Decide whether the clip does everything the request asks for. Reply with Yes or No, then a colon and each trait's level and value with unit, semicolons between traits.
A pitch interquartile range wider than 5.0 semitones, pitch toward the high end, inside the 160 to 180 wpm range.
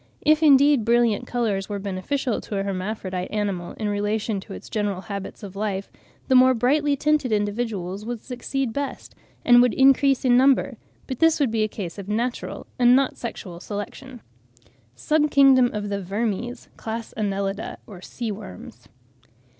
No: average, 4.4 semitones; high, 220 Hz; average, 165 wpm